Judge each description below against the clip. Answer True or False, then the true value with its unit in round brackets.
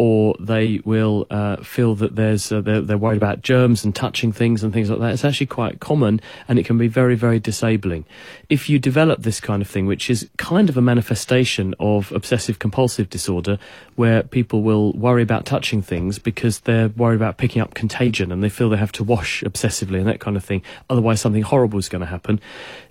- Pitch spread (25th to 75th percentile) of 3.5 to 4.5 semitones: False (2.6 semitones)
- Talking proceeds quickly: True (215 wpm)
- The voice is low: True (110 Hz)